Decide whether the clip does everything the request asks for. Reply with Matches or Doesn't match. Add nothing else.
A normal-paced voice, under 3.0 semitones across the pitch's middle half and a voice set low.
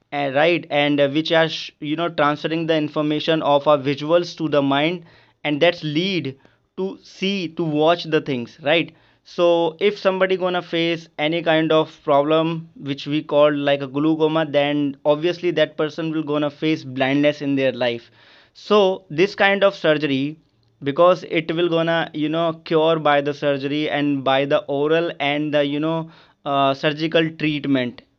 Doesn't match